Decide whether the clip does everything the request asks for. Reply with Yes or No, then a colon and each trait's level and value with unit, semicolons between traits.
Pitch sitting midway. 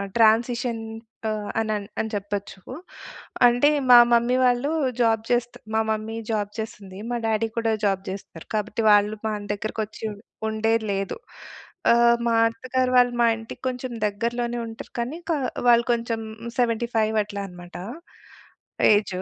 No: high, 225 Hz